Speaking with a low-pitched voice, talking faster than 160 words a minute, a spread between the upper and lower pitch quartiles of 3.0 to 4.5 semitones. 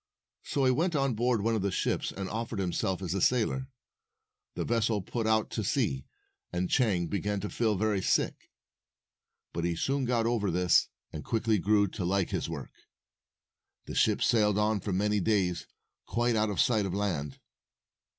Yes: low, 105 Hz; average, 180 wpm; average, 3.5 semitones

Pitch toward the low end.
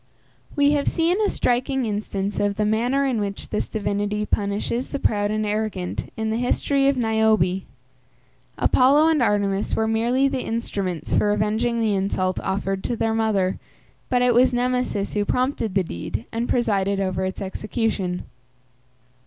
No: high, 220 Hz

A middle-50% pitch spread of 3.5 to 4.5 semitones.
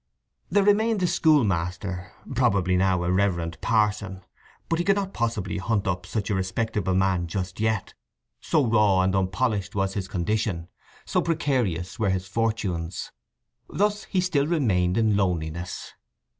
Yes: average, 4.1 semitones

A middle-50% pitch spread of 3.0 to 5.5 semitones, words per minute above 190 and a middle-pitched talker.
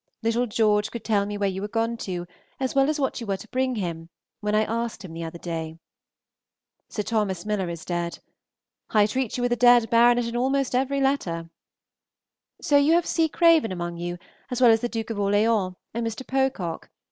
No: average, 4.7 semitones; fast, 205 wpm; high, 225 Hz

